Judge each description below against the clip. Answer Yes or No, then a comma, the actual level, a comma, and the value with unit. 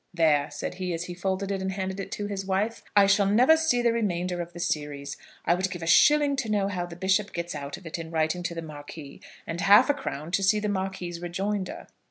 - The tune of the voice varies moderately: Yes, average, 3.1 semitones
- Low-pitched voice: No, high, 190 Hz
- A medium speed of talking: No, fast, 250 wpm